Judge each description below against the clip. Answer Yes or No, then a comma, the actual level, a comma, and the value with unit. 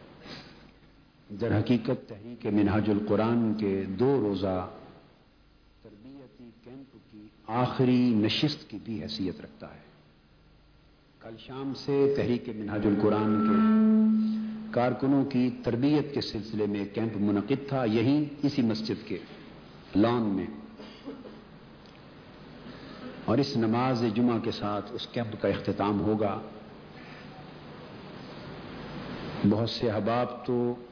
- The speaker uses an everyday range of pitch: Yes, average, 3.6 semitones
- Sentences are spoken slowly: Yes, slow, 105 wpm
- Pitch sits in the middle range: No, low, 115 Hz